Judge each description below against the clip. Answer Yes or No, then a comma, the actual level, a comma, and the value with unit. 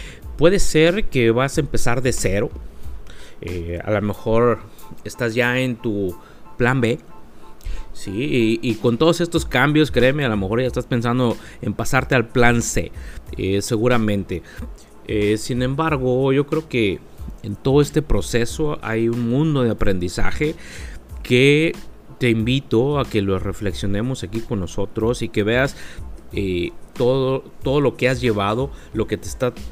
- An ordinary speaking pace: Yes, average, 155 wpm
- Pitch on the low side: Yes, low, 115 Hz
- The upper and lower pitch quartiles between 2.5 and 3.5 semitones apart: No, average, 4.2 semitones